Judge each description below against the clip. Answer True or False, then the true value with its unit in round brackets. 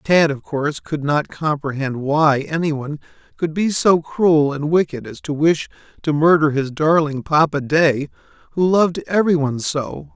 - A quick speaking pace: False (170 wpm)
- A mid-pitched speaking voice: True (155 Hz)